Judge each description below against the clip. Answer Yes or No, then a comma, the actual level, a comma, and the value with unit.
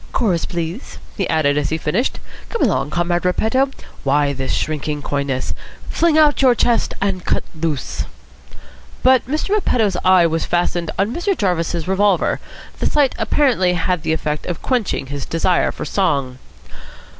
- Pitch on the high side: No, medium, 180 Hz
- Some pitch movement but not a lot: No, wide, 6.9 semitones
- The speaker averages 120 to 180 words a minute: Yes, average, 155 wpm